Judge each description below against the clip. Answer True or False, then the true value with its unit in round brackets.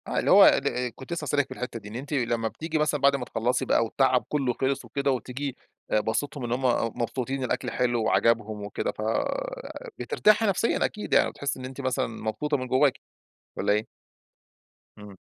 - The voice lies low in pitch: True (130 Hz)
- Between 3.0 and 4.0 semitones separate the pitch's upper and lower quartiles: True (3.3 semitones)